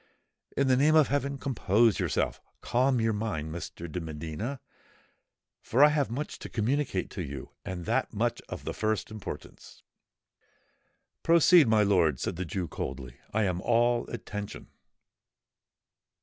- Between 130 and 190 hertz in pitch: No, low, 110 Hz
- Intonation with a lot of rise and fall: Yes, wide, 7.0 semitones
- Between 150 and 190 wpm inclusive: No, slow, 135 wpm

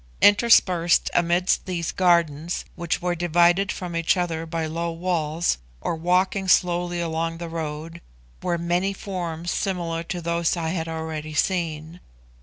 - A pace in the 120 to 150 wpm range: Yes, average, 140 wpm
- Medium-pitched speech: Yes, medium, 170 Hz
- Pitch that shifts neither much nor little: No, narrow, 1.5 semitones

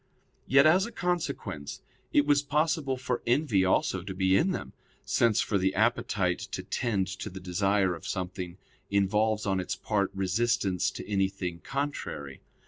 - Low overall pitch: Yes, low, 100 Hz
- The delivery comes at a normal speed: Yes, average, 155 wpm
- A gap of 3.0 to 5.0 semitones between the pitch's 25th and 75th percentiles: No, wide, 5.6 semitones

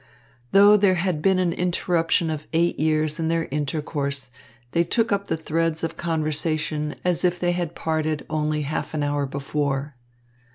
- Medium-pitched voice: Yes, medium, 160 Hz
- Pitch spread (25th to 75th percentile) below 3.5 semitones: Yes, narrow, 2.4 semitones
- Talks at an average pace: Yes, average, 165 wpm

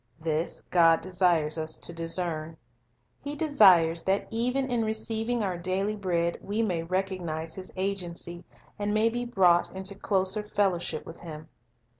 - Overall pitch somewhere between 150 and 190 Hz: Yes, medium, 185 Hz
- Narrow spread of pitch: No, average, 3.9 semitones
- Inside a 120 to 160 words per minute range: Yes, average, 145 wpm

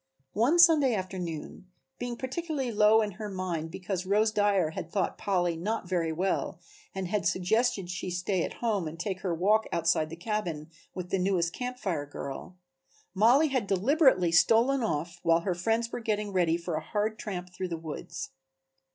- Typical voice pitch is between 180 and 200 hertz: Yes, high, 190 Hz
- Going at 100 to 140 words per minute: No, average, 180 wpm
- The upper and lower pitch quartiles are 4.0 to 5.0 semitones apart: Yes, average, 4.3 semitones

